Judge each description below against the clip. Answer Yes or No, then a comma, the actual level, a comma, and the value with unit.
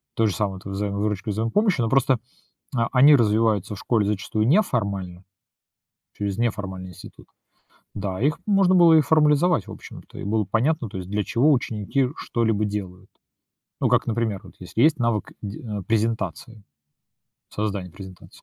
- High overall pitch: No, low, 110 Hz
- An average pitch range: Yes, average, 3.7 semitones